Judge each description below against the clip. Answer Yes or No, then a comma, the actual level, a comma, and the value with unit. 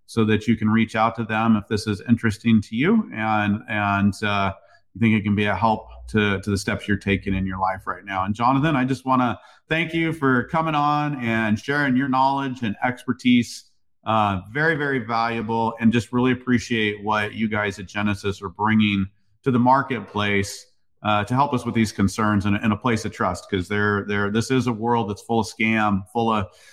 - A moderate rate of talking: No, fast, 215 wpm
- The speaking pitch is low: Yes, low, 110 Hz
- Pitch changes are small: No, average, 3.1 semitones